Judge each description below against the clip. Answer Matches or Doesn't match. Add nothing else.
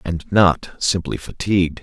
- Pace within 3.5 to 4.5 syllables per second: Matches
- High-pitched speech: Doesn't match